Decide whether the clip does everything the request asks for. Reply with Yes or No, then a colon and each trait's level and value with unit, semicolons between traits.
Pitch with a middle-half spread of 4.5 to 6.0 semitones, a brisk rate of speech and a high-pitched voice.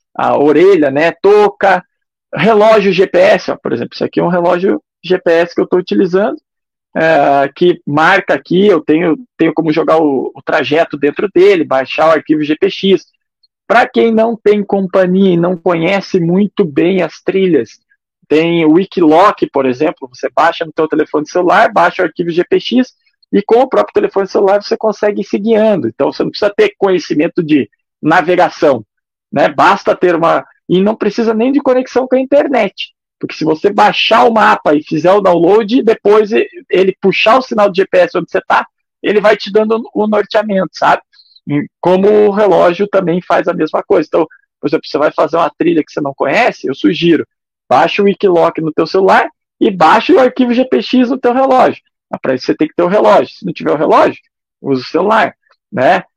Yes: average, 5.2 semitones; fast, 190 wpm; high, 195 Hz